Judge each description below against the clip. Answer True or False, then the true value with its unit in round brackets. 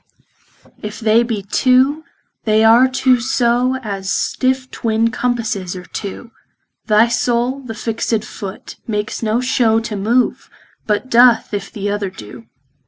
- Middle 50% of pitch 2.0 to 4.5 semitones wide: True (3.0 semitones)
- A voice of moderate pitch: False (225 Hz)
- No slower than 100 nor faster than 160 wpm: True (140 wpm)